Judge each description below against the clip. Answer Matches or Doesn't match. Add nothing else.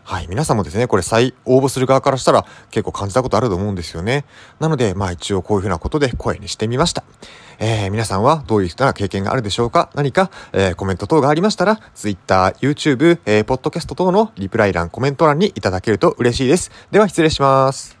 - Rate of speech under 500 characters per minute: Doesn't match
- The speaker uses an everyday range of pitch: Doesn't match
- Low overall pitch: Matches